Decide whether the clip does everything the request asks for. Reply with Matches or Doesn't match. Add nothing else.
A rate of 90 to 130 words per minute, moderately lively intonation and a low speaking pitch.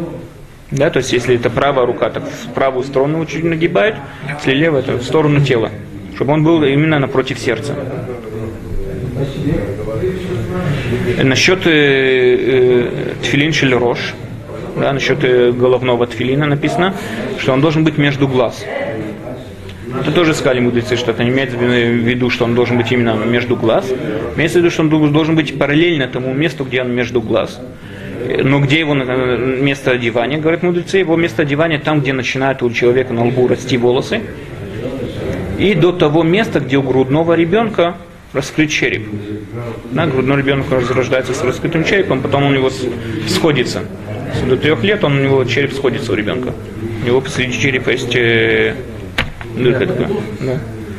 Doesn't match